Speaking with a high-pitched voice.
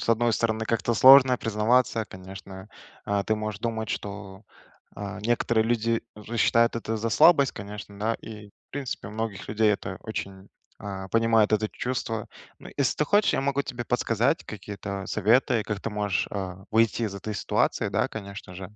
No: low, 110 Hz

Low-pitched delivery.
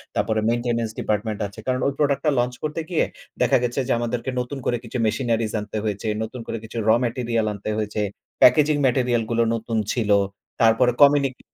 Yes: low, 120 Hz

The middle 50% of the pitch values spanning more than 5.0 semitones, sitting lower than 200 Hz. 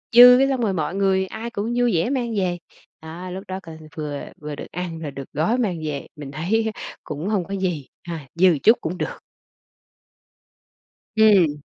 Yes: wide, 5.5 semitones; medium, 185 Hz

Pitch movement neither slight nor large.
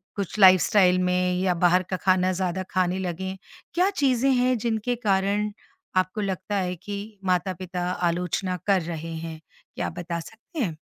No: narrow, 2.2 semitones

